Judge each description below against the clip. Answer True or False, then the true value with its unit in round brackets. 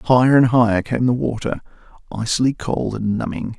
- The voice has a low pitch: True (120 Hz)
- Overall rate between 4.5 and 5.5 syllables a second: True (5.2 syllables/s)